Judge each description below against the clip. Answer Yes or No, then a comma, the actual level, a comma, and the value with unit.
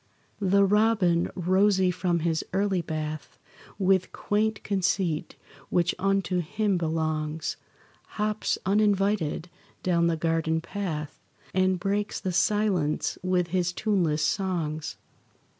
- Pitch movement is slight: No, average, 3.4 semitones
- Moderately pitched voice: Yes, medium, 180 Hz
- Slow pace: Yes, slow, 110 wpm